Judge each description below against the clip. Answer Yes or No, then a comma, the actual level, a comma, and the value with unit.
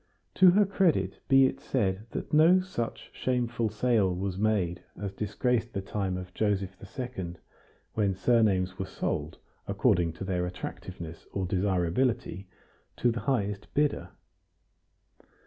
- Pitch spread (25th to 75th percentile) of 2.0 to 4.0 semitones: No, average, 5.0 semitones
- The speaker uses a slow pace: Yes, slow, 130 wpm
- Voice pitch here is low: Yes, low, 100 Hz